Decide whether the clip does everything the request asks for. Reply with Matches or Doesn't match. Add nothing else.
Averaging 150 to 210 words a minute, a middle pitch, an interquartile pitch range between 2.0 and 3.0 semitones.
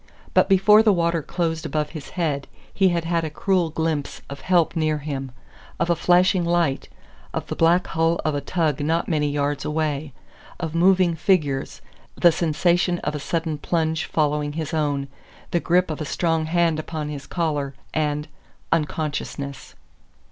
Matches